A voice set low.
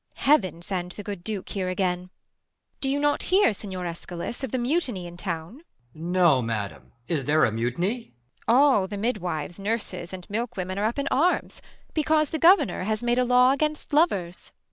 No: high, 200 Hz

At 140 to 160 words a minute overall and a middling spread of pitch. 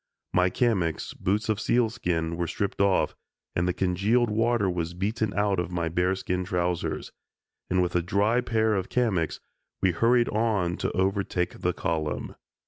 Yes: average, 155 wpm; average, 3.6 semitones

